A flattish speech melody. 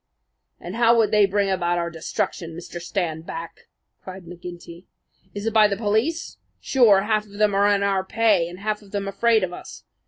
No: average, 3.3 semitones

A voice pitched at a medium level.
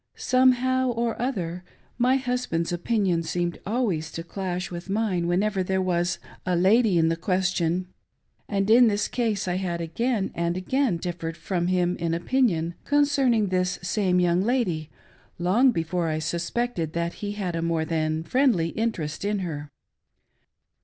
Yes: medium, 180 Hz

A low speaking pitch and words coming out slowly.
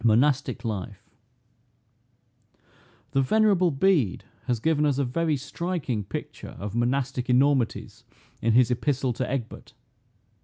Yes: low, 130 Hz; slow, 115 wpm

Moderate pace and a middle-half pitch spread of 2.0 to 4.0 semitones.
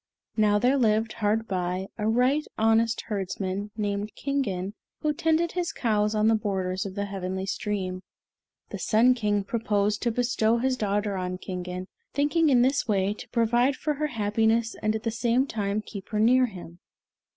Yes: average, 175 wpm; average, 3.4 semitones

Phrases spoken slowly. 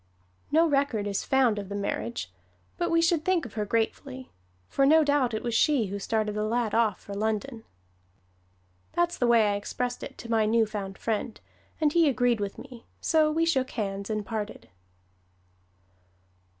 No: average, 175 wpm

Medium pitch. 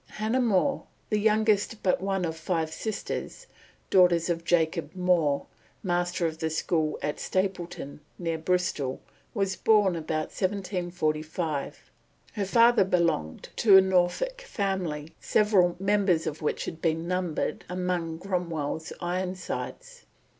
Yes: medium, 180 Hz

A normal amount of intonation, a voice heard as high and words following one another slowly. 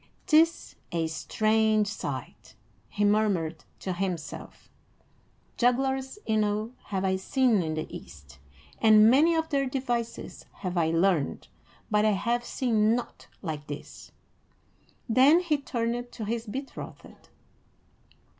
Yes: average, 5.0 semitones; high, 220 Hz; slow, 120 wpm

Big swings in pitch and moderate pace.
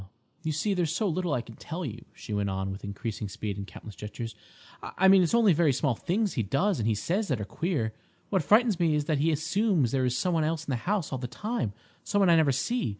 No: wide, 8.2 semitones; fast, 250 wpm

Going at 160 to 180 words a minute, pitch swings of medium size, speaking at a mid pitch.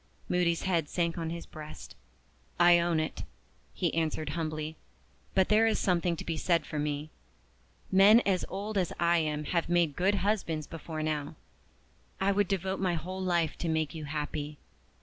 Yes: average, 170 wpm; average, 3.1 semitones; medium, 170 Hz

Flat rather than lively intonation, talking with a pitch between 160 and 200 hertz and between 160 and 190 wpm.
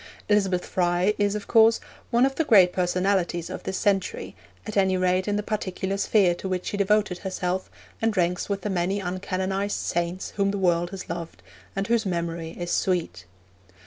Yes: narrow, 2.3 semitones; high, 190 Hz; average, 180 wpm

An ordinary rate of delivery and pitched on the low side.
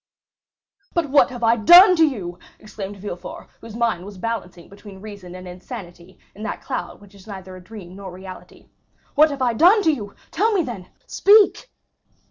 No: average, 180 wpm; high, 210 Hz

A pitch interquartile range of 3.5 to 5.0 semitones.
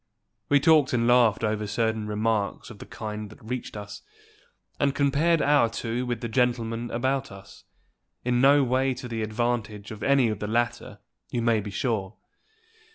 No: average, 3.0 semitones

